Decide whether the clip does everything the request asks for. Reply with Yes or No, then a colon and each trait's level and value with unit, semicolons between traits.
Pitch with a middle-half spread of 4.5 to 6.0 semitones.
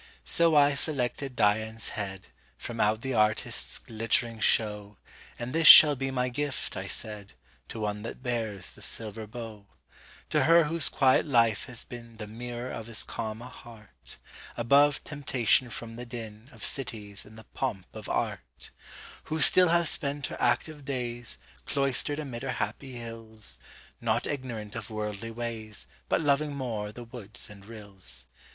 No: average, 3.8 semitones